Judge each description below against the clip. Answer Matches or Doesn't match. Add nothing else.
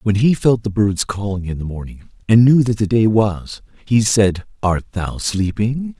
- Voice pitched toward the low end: Matches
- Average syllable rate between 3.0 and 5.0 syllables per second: Matches